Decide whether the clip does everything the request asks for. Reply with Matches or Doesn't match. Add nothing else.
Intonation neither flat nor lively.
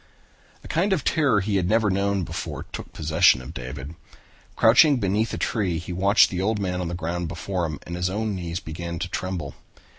Matches